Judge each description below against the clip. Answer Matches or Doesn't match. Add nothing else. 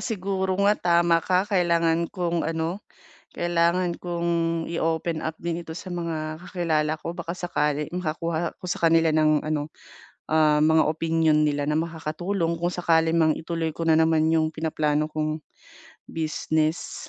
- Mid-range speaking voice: Matches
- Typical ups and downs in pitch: Doesn't match